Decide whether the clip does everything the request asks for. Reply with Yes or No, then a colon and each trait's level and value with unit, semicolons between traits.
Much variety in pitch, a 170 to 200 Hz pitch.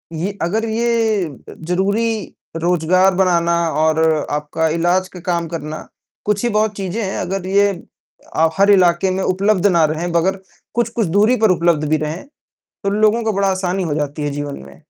No: average, 3.6 semitones; medium, 185 Hz